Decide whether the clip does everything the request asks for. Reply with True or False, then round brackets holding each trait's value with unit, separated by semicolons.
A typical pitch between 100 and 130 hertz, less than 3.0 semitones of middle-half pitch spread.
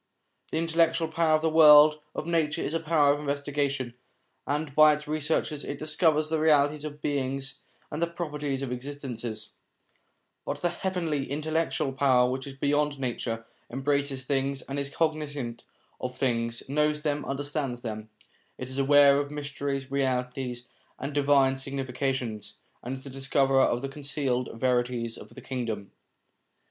False (140 Hz; 2.4 semitones)